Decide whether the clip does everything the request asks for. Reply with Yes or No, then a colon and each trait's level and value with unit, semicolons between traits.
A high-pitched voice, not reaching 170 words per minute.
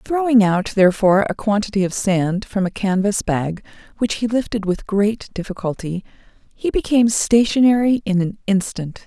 Yes: high, 205 Hz; average, 150 wpm